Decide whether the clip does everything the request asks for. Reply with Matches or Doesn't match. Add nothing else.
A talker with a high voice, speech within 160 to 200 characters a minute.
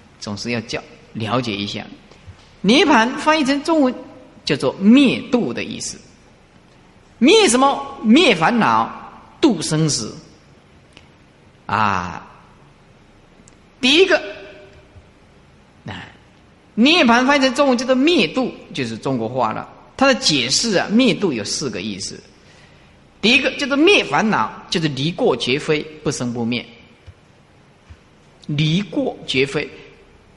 Matches